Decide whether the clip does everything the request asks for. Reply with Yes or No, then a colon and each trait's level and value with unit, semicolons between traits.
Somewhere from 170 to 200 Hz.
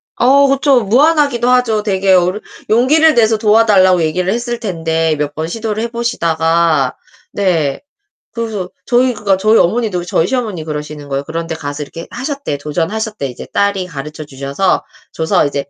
Yes: high, 195 Hz